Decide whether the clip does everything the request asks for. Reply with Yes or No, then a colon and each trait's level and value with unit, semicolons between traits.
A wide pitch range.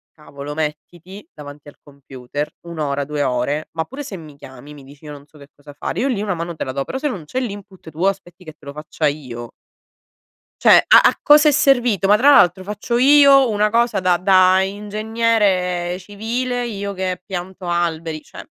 Yes: wide, 6.0 semitones